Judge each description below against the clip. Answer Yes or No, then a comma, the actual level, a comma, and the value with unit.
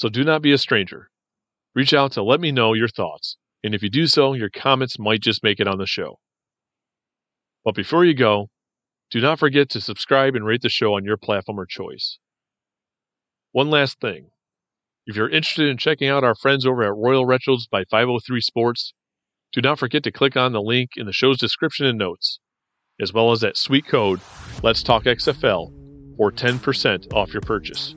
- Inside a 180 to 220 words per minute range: Yes, average, 195 wpm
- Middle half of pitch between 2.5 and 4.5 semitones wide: Yes, average, 3.8 semitones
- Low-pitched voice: Yes, low, 125 Hz